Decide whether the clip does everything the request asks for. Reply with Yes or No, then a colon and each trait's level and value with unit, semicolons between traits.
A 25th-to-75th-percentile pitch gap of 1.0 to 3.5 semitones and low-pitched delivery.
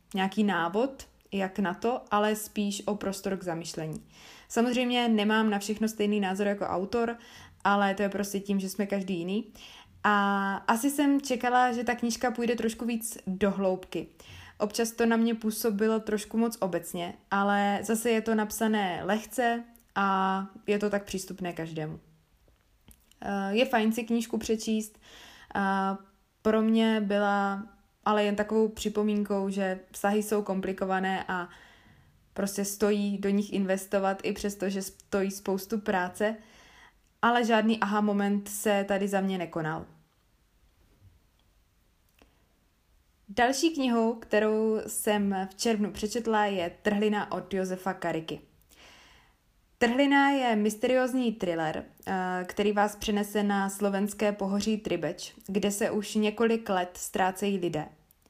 No: narrow, 2.5 semitones; high, 205 Hz